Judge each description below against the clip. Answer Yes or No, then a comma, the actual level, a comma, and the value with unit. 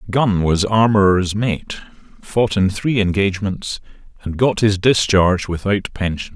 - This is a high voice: No, low, 100 Hz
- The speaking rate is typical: No, slow, 130 wpm